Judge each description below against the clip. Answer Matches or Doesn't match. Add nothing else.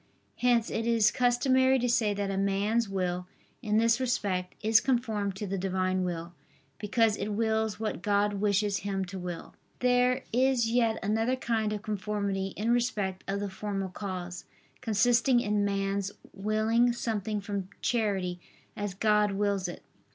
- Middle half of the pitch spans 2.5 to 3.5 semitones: Matches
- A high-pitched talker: Matches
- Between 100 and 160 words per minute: Matches